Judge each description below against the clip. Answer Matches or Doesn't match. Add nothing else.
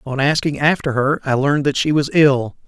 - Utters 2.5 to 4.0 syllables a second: Doesn't match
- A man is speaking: Matches